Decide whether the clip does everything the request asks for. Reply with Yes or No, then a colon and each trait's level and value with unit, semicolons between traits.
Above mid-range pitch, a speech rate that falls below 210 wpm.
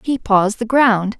Yes: high, 225 Hz; average, 200 wpm